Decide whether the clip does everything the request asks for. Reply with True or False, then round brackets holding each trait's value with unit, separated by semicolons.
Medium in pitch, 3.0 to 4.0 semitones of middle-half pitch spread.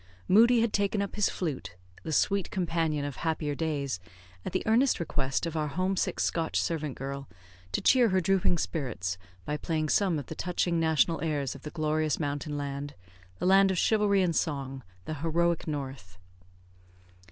False (160 Hz; 4.4 semitones)